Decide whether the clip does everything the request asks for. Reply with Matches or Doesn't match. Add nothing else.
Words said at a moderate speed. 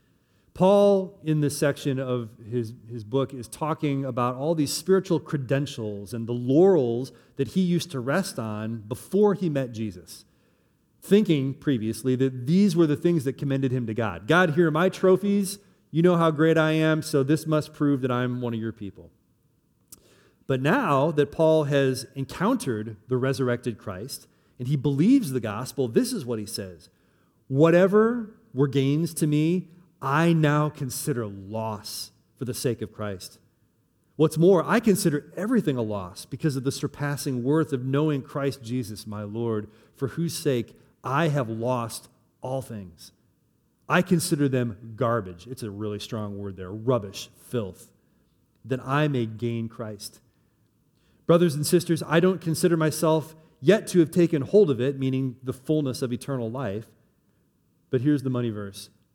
Matches